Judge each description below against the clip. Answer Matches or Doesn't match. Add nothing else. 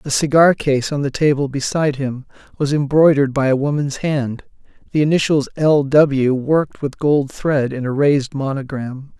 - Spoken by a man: Matches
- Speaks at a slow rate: Doesn't match